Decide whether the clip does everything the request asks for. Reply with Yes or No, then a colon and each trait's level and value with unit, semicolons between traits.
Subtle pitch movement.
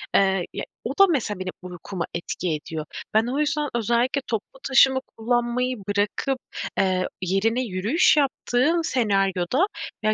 No: wide, 5.4 semitones